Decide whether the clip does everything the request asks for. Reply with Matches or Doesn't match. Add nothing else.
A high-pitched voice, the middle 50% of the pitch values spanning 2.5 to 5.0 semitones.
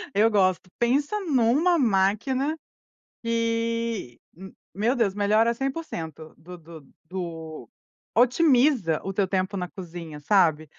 Doesn't match